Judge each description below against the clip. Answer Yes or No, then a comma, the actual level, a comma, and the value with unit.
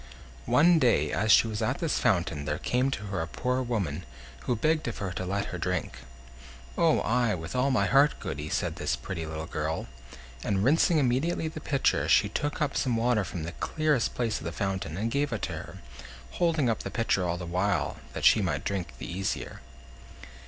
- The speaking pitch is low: Yes, low, 110 Hz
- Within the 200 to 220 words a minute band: Yes, fast, 205 wpm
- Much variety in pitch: Yes, wide, 7.2 semitones